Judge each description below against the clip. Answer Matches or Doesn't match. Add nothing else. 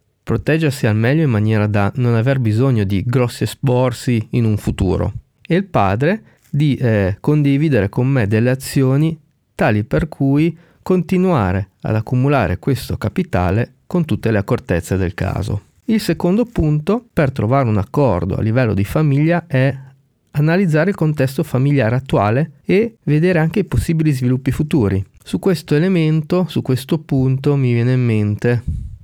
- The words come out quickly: Doesn't match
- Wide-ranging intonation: Matches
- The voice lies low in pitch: Matches